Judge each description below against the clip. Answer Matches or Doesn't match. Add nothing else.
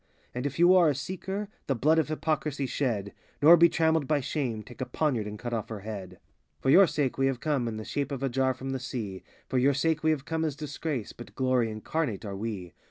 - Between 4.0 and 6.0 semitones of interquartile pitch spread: Matches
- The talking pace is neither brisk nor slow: Doesn't match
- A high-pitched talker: Doesn't match